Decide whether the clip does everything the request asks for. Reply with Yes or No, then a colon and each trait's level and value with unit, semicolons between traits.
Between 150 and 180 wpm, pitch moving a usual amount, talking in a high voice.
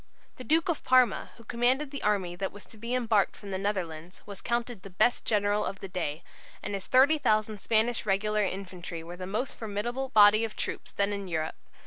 No: average, 200 wpm; average, 3.8 semitones; high, 210 Hz